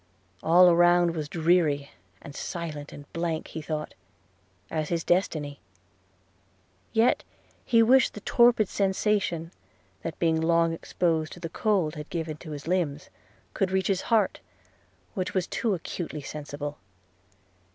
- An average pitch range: Yes, average, 3.3 semitones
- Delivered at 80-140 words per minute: Yes, slow, 135 wpm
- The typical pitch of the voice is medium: Yes, medium, 170 Hz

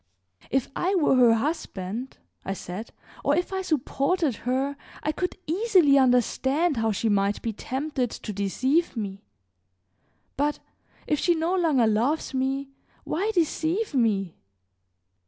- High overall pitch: Yes, very high, 270 Hz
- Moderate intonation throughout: No, wide, 6.0 semitones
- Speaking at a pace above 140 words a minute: No, slow, 135 wpm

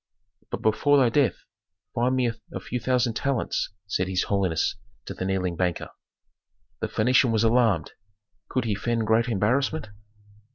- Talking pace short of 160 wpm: Yes, average, 150 wpm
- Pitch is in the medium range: No, low, 115 Hz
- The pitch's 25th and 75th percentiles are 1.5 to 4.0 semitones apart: No, average, 4.5 semitones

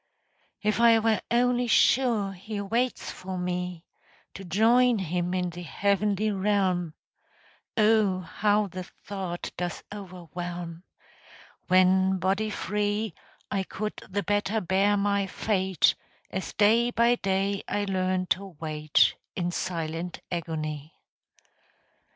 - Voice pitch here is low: No, high, 195 Hz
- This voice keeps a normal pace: No, slow, 115 wpm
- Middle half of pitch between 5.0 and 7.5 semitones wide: No, average, 2.8 semitones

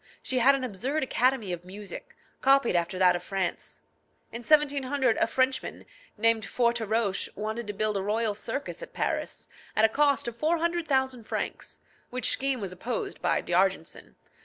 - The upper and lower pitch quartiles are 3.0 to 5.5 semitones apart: Yes, average, 5.1 semitones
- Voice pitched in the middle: No, high, 230 Hz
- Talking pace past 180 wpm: No, average, 160 wpm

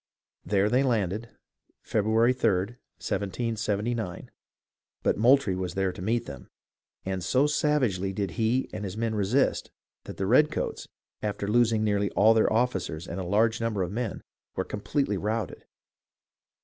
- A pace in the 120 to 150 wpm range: Yes, average, 145 wpm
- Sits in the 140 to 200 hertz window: No, low, 105 Hz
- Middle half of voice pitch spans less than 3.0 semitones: No, average, 3.4 semitones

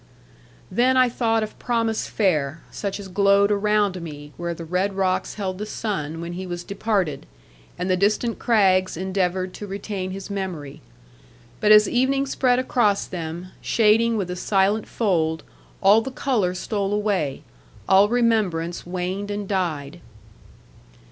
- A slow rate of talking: No, average, 150 wpm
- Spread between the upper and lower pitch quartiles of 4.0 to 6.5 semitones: No, average, 3.1 semitones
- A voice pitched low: No, high, 195 Hz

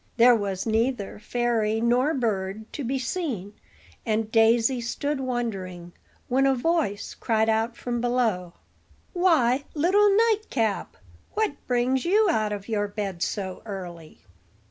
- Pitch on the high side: Yes, high, 235 Hz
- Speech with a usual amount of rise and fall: Yes, average, 4.3 semitones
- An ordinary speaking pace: No, slow, 130 wpm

